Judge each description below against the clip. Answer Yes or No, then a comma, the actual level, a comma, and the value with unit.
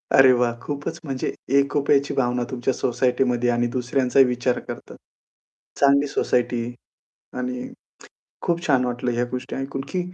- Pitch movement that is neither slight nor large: No, narrow, 2.0 semitones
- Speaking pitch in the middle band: No, low, 125 Hz